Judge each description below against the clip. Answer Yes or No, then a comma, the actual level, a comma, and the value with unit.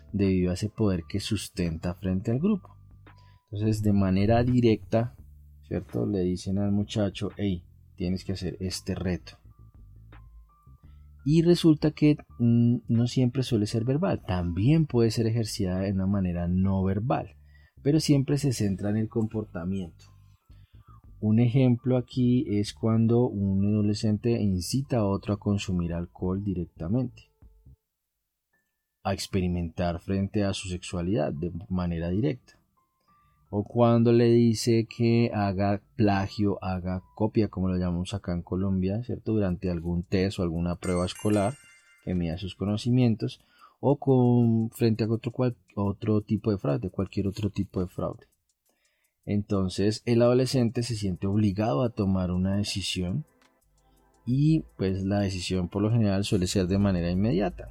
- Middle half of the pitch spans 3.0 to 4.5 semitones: Yes, average, 3.8 semitones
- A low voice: Yes, low, 100 Hz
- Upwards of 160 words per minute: No, average, 140 wpm